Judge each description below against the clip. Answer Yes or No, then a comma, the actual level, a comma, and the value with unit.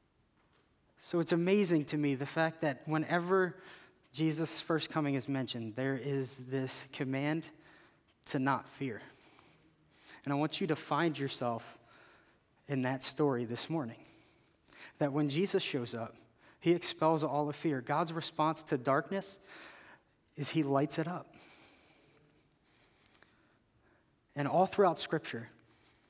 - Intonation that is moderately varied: Yes, average, 3.3 semitones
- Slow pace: Yes, slow, 130 wpm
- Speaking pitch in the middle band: Yes, medium, 150 Hz